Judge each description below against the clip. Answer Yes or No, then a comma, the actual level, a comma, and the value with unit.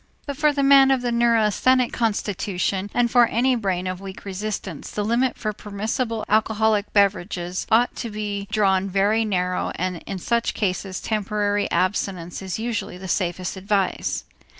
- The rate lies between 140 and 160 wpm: Yes, average, 150 wpm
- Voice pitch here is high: Yes, high, 205 Hz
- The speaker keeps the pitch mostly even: No, average, 3.4 semitones